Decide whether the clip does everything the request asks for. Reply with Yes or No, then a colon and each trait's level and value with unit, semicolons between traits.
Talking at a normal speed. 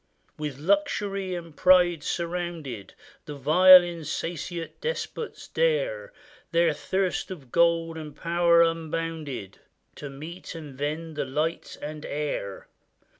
No: slow, 115 wpm